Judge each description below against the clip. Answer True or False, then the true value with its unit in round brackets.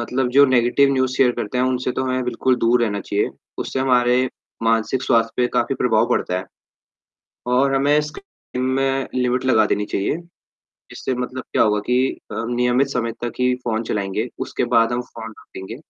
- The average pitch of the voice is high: False (125 Hz)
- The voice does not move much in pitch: True (2.2 semitones)